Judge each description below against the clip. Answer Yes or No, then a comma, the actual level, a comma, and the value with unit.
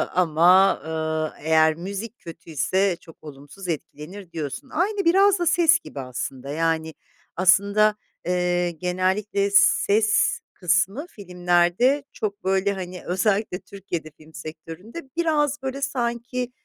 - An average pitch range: No, wide, 5.7 semitones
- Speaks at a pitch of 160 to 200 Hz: Yes, medium, 185 Hz